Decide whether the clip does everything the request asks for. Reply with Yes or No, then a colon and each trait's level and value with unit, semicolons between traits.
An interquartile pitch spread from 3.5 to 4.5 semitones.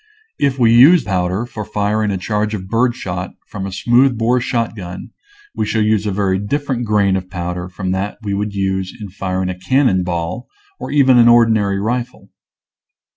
Yes: average, 4.0 semitones